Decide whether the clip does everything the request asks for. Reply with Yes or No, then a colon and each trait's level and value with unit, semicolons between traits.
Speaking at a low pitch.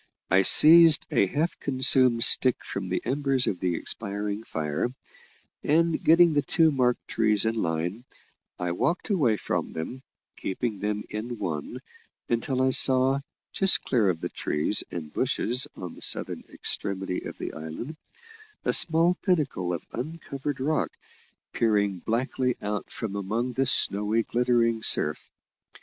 Yes: low, 115 Hz